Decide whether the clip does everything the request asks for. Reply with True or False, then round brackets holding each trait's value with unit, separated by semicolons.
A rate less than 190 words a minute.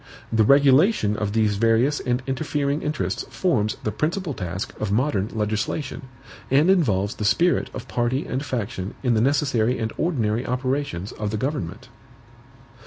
True (150 wpm)